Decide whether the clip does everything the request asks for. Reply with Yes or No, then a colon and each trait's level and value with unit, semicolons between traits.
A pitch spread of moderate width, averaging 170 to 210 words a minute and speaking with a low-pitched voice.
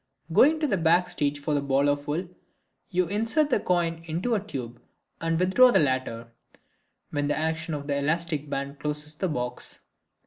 No: average, 4.2 semitones; average, 195 wpm; medium, 155 Hz